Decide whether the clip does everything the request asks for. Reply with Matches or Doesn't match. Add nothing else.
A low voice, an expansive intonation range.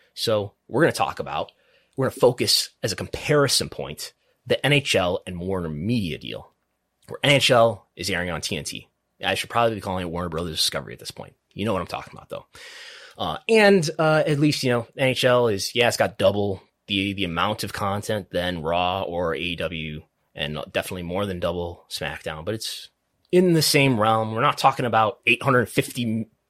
Matches